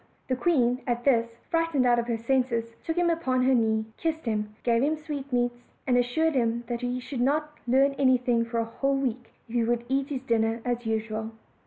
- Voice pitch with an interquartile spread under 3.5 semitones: Yes, average, 2.9 semitones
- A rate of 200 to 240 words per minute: Yes, fast, 205 wpm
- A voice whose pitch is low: No, high, 245 Hz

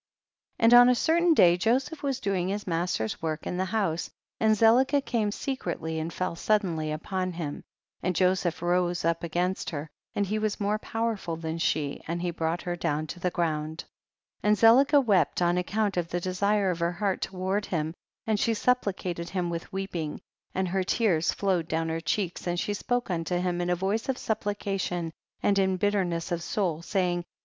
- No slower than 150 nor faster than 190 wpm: No, average, 200 wpm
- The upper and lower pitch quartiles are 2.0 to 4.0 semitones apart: Yes, average, 3.5 semitones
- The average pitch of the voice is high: No, medium, 180 Hz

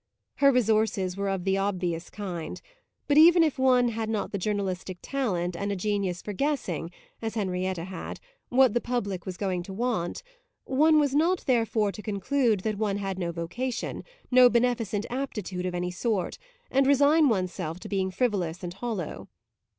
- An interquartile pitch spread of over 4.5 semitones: Yes, average, 5.2 semitones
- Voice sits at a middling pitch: No, high, 205 Hz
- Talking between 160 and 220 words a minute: Yes, average, 175 wpm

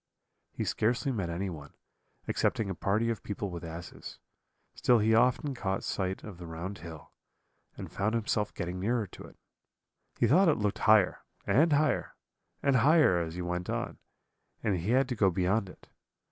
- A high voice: No, low, 105 Hz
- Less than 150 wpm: No, average, 175 wpm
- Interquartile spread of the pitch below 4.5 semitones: No, average, 4.8 semitones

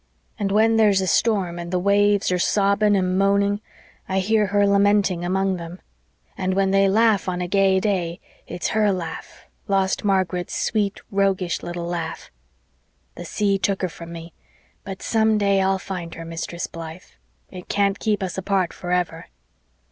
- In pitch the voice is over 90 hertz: Yes, high, 190 Hz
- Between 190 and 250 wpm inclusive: No, average, 165 wpm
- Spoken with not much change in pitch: Yes, narrow, 2.2 semitones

